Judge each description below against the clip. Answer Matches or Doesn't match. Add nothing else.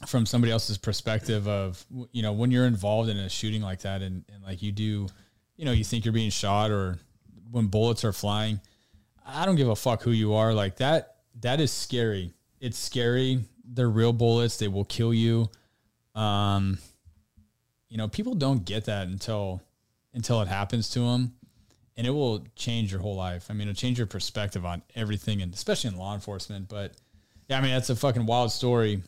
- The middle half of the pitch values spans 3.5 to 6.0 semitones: Doesn't match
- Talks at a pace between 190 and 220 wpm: Matches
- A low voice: Matches